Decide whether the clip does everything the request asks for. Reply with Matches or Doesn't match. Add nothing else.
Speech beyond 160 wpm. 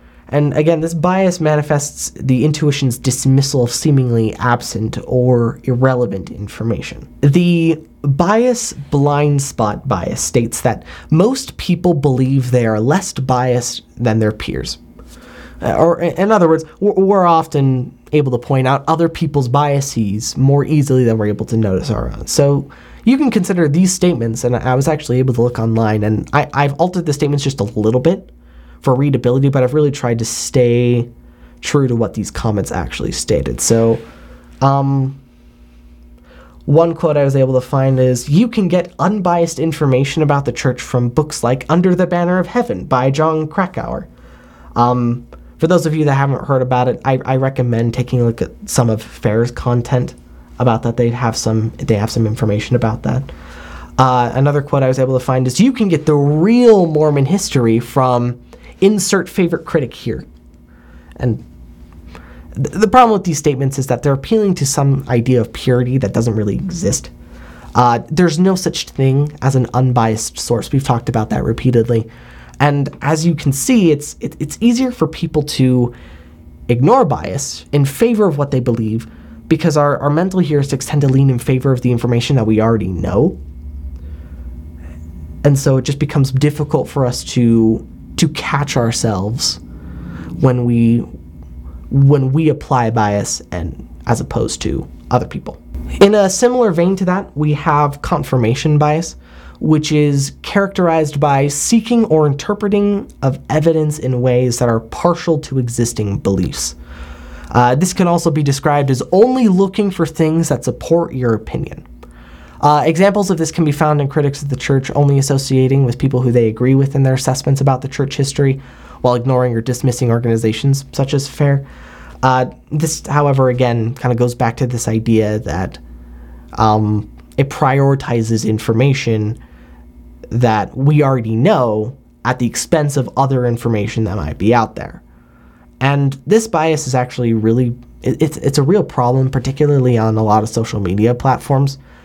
Matches